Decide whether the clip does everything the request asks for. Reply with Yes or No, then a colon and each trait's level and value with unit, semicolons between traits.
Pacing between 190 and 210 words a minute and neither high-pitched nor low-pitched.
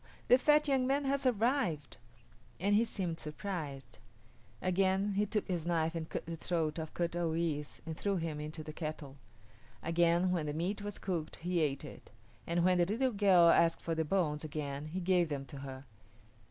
Yes: average, 195 wpm; medium, 170 Hz